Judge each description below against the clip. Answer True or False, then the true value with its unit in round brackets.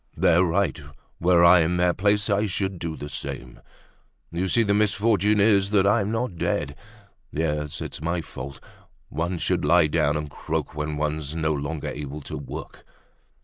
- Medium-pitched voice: False (85 Hz)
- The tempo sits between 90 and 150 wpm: False (170 wpm)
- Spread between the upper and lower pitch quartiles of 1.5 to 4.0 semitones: False (4.8 semitones)